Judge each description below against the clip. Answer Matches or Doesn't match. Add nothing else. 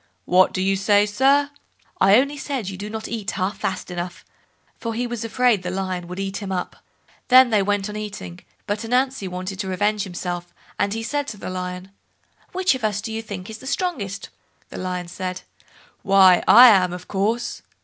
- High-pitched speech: Matches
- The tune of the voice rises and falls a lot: Doesn't match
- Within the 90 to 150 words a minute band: Doesn't match